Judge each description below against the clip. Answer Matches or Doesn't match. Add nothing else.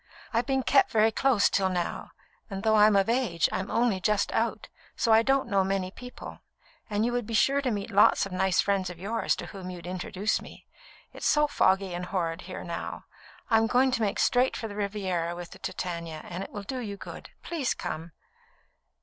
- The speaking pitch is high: Matches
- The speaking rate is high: Matches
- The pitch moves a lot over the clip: Doesn't match